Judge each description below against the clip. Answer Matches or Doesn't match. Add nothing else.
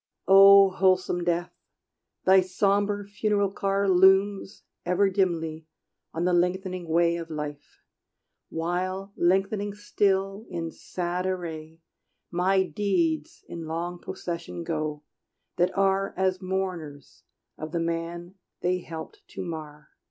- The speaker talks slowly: Matches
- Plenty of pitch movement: Doesn't match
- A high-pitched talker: Doesn't match